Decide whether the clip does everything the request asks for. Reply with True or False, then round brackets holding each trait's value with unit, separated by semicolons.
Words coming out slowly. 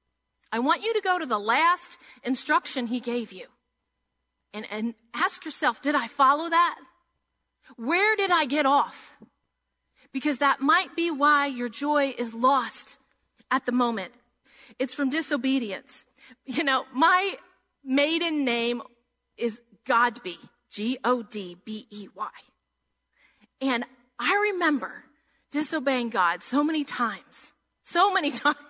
True (125 wpm)